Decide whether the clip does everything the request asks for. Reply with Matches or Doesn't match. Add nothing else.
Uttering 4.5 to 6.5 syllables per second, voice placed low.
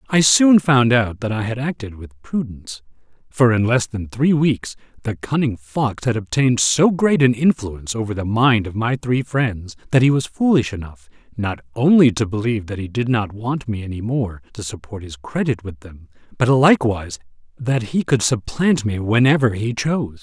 Matches